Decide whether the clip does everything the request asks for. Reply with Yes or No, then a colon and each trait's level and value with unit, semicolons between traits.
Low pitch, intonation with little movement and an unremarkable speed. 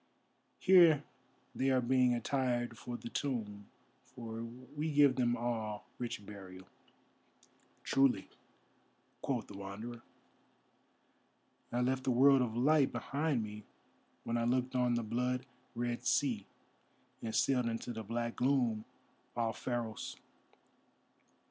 No: low, 120 Hz; narrow, 2.3 semitones; slow, 120 wpm